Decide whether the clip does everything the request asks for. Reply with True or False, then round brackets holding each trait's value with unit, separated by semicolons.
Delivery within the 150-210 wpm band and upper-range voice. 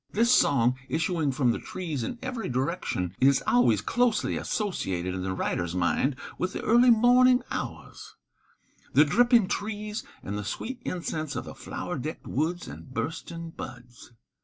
False (155 wpm; 160 Hz)